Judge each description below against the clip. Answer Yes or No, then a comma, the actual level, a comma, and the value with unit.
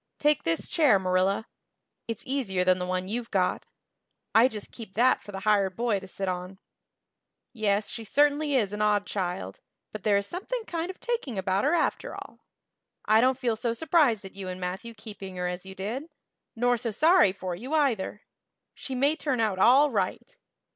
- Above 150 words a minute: Yes, average, 190 wpm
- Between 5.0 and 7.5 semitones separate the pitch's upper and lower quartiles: Yes, wide, 5.5 semitones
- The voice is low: No, high, 215 Hz